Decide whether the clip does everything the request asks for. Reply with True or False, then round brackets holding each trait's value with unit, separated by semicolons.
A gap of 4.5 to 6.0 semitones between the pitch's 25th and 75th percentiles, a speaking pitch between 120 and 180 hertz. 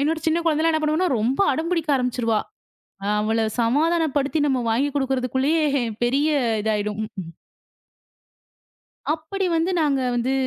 False (5.1 semitones; 275 Hz)